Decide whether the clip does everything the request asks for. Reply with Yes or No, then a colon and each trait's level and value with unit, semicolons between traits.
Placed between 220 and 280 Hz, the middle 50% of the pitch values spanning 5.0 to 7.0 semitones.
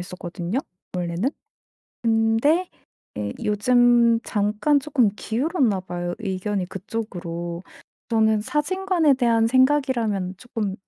Yes: high, 225 Hz; wide, 5.5 semitones